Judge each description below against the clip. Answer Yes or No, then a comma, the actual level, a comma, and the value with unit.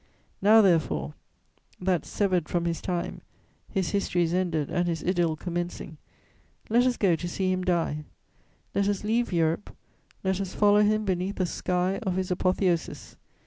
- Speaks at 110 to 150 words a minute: No, average, 160 wpm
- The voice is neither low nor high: Yes, medium, 180 Hz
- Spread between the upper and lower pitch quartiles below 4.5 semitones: Yes, narrow, 2.5 semitones